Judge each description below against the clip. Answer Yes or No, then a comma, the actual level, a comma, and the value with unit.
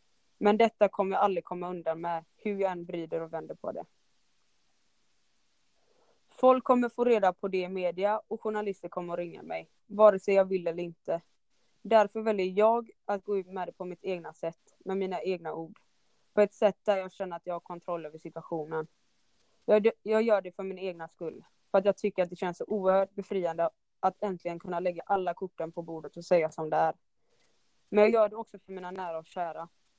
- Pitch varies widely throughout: No, average, 3.1 semitones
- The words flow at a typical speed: No, fast, 210 wpm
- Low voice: No, medium, 185 Hz